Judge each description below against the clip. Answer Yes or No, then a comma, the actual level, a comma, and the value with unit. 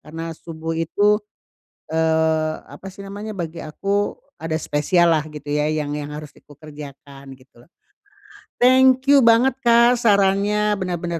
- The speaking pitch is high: No, medium, 165 Hz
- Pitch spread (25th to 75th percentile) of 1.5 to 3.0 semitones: No, average, 5.3 semitones